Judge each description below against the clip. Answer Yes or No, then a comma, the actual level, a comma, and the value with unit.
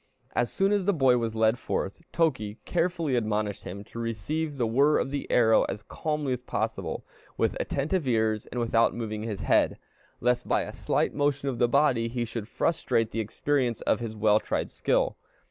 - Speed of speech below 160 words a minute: No, average, 190 wpm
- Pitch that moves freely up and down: No, average, 4.4 semitones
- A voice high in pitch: No, low, 120 Hz